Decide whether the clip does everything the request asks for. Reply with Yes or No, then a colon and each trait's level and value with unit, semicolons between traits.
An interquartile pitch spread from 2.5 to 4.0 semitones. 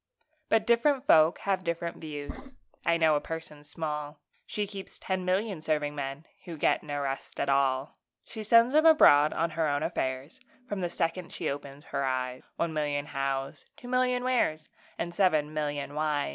No: average, 4.8 semitones